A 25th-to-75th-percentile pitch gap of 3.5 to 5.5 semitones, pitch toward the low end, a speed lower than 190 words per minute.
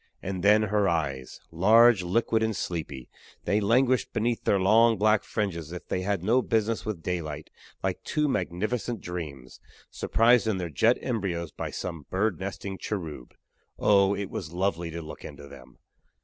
Yes: average, 4.5 semitones; very low, 95 Hz; average, 165 wpm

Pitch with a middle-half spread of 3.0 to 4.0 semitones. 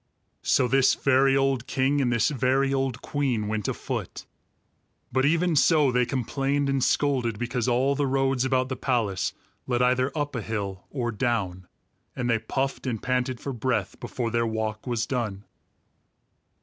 No: narrow, 2.6 semitones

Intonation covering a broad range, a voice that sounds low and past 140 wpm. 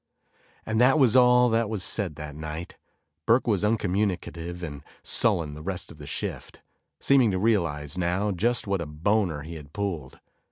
Yes: wide, 5.9 semitones; very low, 95 Hz; average, 170 wpm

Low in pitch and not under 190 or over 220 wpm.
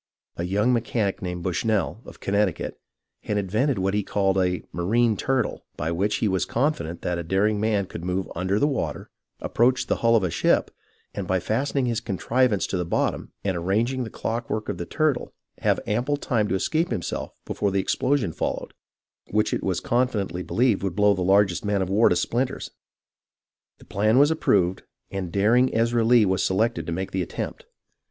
Yes: low, 105 Hz; average, 195 wpm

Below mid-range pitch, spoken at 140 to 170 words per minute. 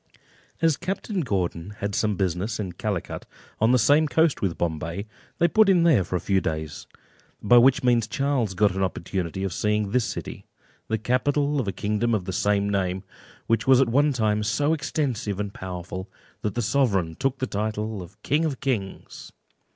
No: low, 105 Hz; average, 185 wpm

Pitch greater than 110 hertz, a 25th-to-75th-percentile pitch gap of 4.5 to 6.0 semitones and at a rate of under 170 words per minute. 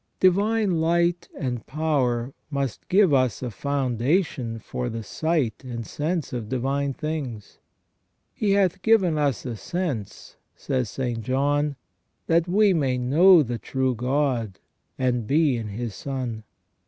Yes: low, 135 Hz; average, 5.2 semitones; average, 140 wpm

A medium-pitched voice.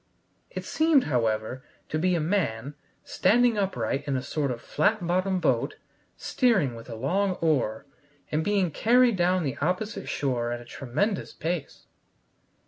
Yes: medium, 165 Hz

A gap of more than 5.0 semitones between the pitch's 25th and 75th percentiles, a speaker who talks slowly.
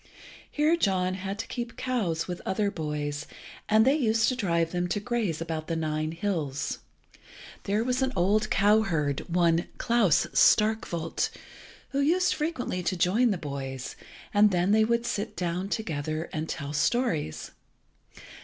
No: wide, 5.5 semitones; average, 150 wpm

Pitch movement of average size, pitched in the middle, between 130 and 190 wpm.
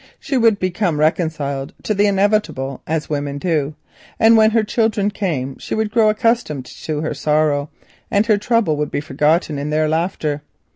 No: wide, 6.2 semitones; medium, 160 Hz; average, 175 wpm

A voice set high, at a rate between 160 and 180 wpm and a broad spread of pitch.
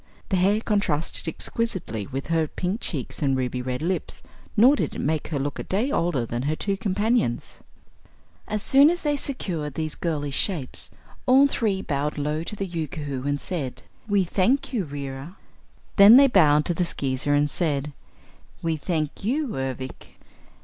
No: medium, 165 Hz; average, 170 wpm; wide, 6.2 semitones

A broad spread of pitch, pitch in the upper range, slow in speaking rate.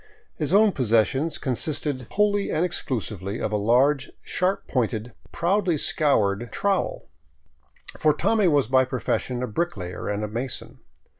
No: wide, 6.9 semitones; low, 135 Hz; slow, 130 wpm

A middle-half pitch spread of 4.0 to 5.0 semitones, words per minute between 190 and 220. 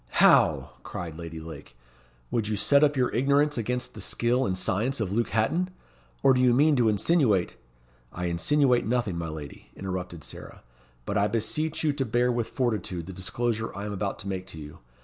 No: wide, 5.5 semitones; average, 195 wpm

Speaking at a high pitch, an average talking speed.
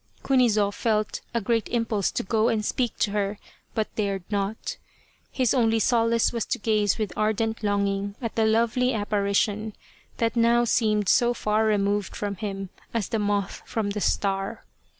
Yes: high, 215 Hz; average, 165 wpm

